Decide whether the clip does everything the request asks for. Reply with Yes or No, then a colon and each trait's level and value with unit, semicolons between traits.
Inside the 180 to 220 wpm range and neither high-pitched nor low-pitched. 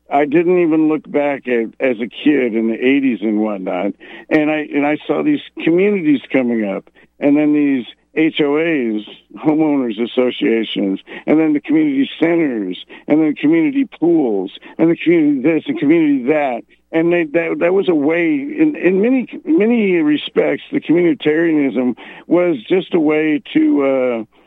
No: average, 160 wpm; medium, 160 Hz